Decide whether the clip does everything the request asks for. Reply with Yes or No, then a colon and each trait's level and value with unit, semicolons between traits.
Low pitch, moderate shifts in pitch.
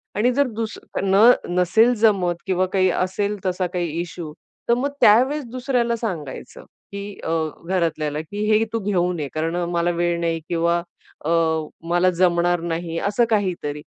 No: medium, 180 Hz; average, 3.7 semitones